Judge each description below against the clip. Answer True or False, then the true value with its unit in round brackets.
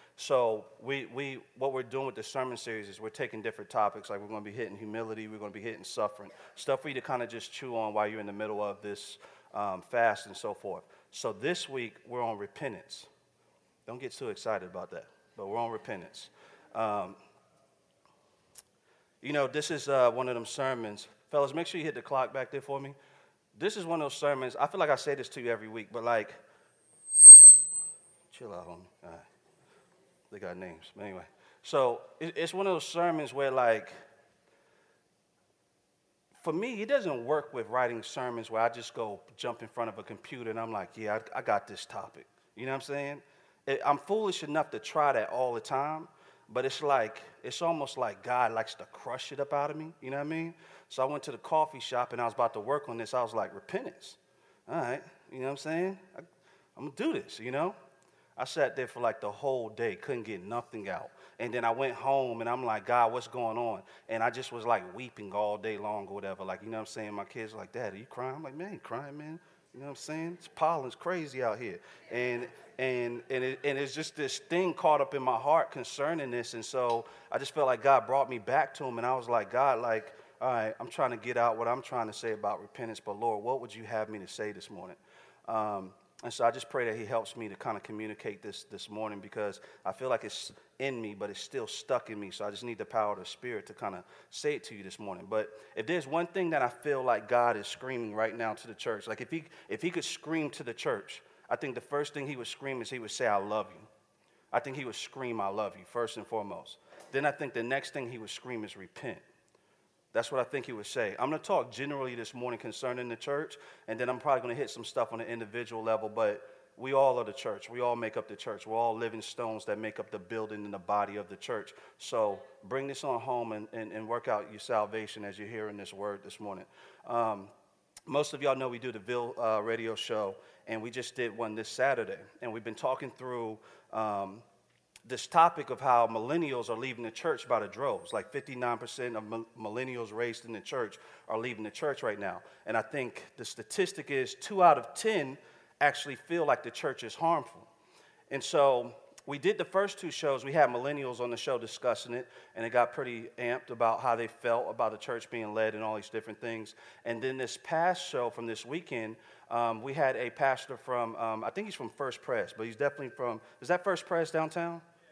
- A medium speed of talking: False (240 wpm)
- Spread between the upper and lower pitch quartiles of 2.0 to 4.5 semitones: True (4.1 semitones)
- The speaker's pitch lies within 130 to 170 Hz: False (120 Hz)